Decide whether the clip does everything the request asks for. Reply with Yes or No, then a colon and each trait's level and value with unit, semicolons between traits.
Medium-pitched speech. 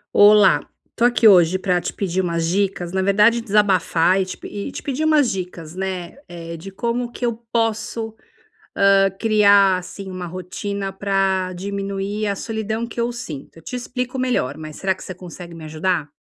No: high, 195 Hz